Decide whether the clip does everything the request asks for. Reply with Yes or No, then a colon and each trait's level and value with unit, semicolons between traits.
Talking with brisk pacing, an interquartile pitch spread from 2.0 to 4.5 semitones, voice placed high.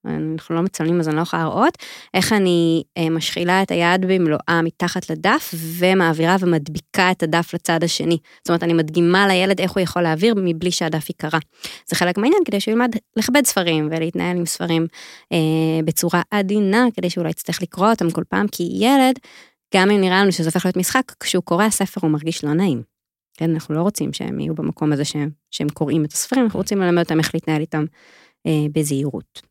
No: fast, 195 wpm; average, 3.1 semitones; medium, 170 Hz